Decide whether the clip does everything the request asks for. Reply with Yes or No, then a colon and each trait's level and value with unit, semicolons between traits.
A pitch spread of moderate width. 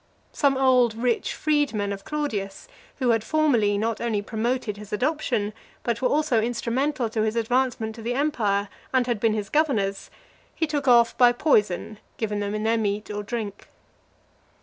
Yes: average, 3.7 semitones